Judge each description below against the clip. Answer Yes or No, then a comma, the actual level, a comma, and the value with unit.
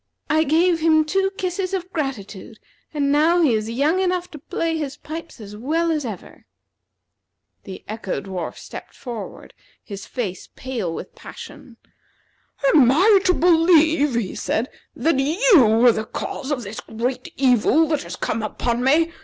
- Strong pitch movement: Yes, wide, 6.3 semitones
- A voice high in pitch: Yes, very high, 280 Hz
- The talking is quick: No, average, 160 wpm